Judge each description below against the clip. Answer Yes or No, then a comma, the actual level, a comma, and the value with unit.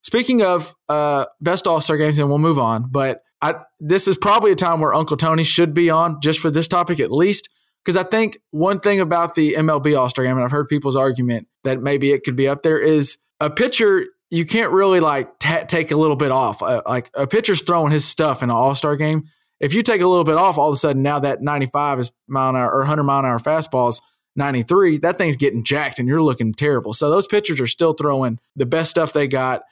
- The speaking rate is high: Yes, fast, 245 wpm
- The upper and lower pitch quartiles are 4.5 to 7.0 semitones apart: No, average, 3.8 semitones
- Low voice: No, medium, 150 Hz